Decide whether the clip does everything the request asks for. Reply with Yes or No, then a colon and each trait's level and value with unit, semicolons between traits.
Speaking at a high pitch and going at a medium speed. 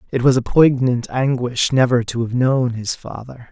No: low, 125 Hz; average, 190 wpm